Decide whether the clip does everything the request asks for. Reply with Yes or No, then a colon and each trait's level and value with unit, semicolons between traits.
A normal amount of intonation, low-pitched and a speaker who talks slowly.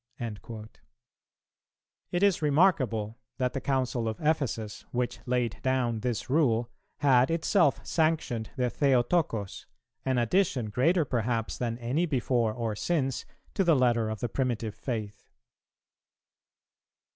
Yes: average, 3.9 semitones; low, 125 Hz; slow, 120 wpm